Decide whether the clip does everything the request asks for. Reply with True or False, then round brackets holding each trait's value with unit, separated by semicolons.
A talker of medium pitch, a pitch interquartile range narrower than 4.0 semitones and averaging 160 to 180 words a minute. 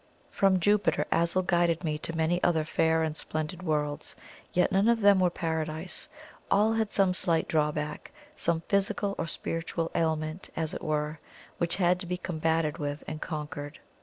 True (165 Hz; 2.8 semitones; 165 wpm)